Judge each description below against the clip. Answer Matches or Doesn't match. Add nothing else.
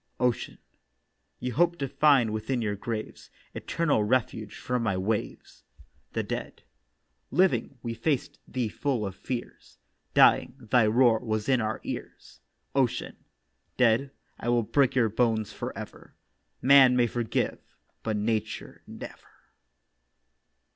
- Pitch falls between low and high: Doesn't match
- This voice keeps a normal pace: Doesn't match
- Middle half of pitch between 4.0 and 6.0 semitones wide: Doesn't match